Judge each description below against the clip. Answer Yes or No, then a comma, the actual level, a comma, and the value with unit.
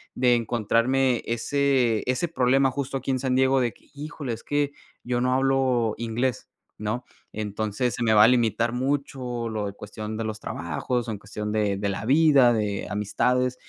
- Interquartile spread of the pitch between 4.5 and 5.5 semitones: No, average, 3.3 semitones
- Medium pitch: No, low, 120 Hz